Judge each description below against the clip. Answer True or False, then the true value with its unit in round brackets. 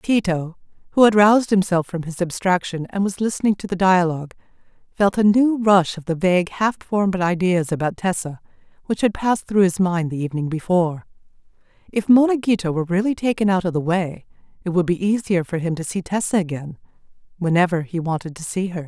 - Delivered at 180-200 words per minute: True (190 wpm)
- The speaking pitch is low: False (185 Hz)